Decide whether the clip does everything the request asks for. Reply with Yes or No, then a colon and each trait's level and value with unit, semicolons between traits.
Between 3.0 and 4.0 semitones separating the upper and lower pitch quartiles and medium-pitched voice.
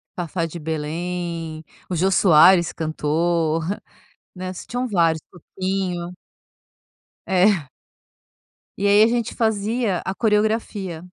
Yes: average, 3.5 semitones; medium, 180 Hz